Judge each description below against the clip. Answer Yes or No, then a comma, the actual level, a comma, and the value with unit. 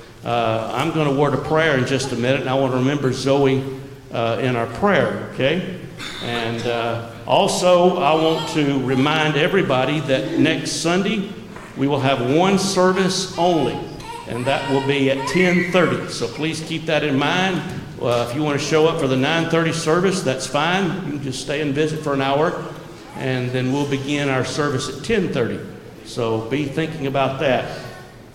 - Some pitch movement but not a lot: Yes, average, 3.6 semitones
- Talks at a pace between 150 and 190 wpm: Yes, average, 180 wpm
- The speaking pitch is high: No, medium, 140 Hz